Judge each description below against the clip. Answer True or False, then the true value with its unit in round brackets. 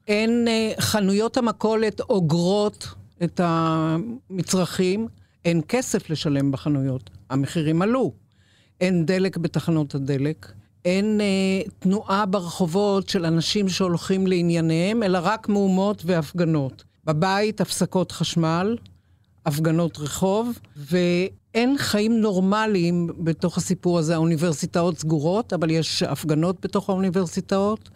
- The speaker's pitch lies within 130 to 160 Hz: False (180 Hz)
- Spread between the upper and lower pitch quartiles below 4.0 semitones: True (3.6 semitones)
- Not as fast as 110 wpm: True (100 wpm)